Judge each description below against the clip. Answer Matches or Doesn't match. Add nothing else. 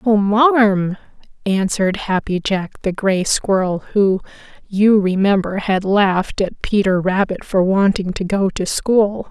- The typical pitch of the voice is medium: Doesn't match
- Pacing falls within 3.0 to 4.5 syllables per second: Matches